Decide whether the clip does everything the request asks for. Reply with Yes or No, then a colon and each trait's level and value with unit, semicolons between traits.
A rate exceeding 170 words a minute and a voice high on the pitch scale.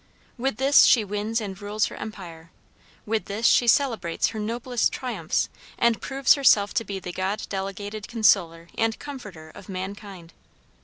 No: average, 155 wpm; high, 210 Hz